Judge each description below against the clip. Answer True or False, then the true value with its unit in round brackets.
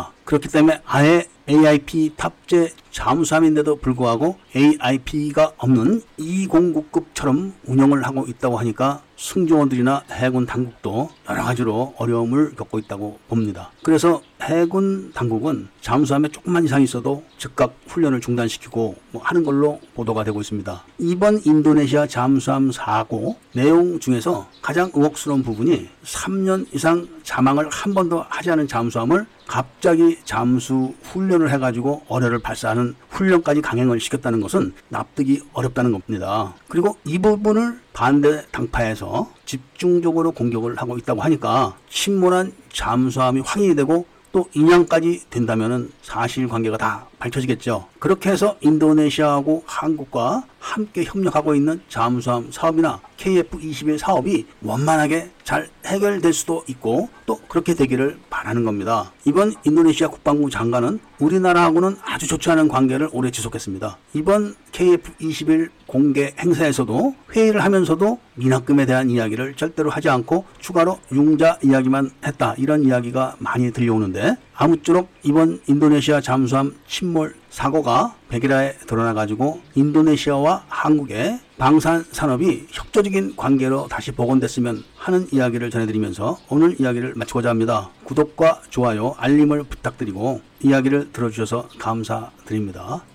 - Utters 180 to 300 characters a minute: False (340 characters per minute)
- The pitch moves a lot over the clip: False (4.9 semitones)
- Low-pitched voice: False (145 Hz)